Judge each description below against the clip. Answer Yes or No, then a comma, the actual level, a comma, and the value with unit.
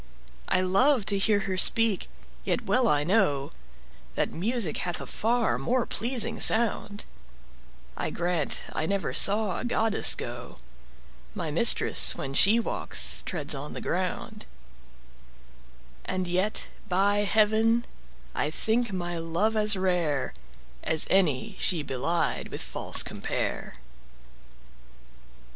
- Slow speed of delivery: Yes, slow, 120 wpm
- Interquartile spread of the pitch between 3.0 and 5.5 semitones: Yes, average, 4.2 semitones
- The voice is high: Yes, high, 195 Hz